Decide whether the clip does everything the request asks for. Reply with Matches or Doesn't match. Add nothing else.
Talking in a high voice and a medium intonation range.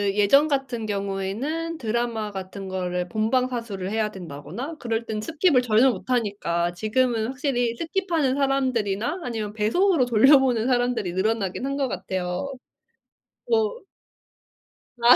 Matches